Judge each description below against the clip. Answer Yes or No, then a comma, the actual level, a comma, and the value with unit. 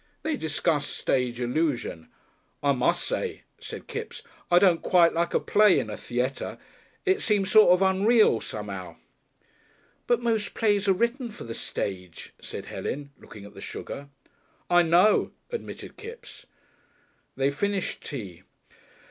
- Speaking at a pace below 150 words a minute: Yes, average, 140 wpm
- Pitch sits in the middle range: Yes, medium, 170 Hz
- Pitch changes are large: Yes, wide, 9.0 semitones